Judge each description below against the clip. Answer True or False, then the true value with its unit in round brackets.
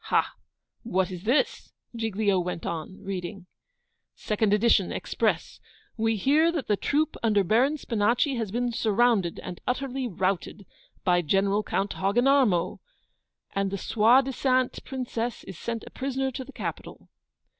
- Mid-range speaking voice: False (220 Hz)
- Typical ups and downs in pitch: True (4.7 semitones)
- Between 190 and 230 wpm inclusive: False (135 wpm)